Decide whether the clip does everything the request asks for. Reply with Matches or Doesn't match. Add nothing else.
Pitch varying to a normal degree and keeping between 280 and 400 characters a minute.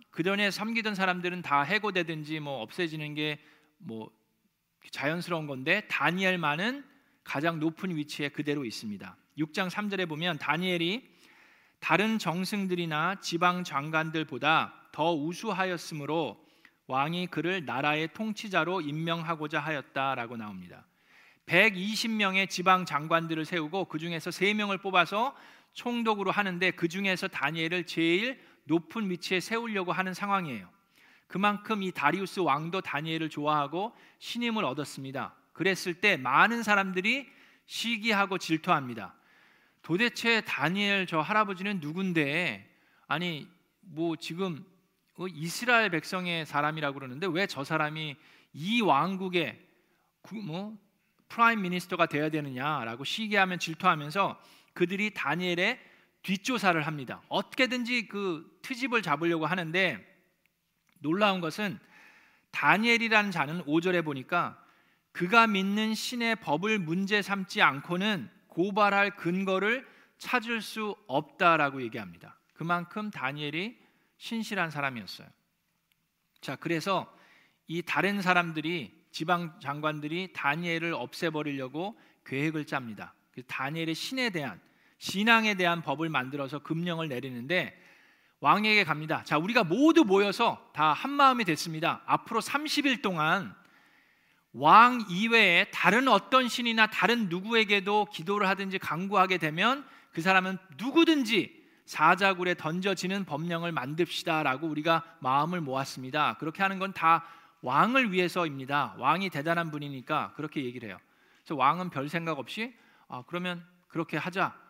Matches